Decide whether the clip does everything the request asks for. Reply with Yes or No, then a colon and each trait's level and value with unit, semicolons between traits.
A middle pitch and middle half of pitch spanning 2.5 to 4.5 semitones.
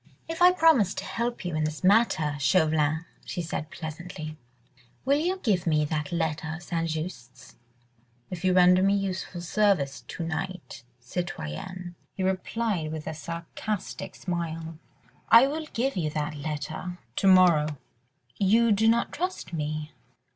Yes: medium, 175 Hz; average, 4.1 semitones